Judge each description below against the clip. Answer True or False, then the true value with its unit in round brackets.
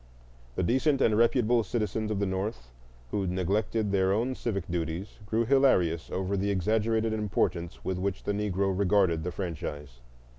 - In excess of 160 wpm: False (155 wpm)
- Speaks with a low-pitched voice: True (100 Hz)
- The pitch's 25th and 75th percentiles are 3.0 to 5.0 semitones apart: True (3.4 semitones)